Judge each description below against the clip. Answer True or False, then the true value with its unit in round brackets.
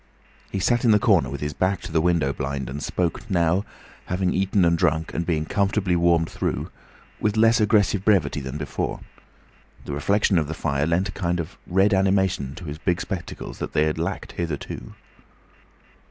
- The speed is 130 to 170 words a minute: False (185 wpm)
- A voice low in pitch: True (85 Hz)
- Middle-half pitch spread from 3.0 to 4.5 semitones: True (4.0 semitones)